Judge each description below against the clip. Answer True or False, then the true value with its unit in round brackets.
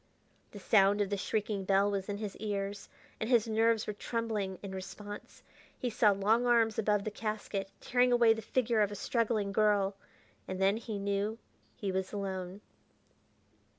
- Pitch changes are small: True (2.1 semitones)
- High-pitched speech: True (205 Hz)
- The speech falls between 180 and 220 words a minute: False (170 wpm)